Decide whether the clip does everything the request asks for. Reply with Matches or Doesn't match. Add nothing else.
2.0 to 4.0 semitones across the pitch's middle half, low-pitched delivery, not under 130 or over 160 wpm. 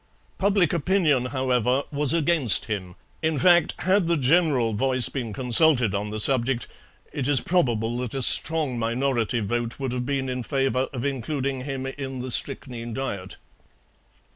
Matches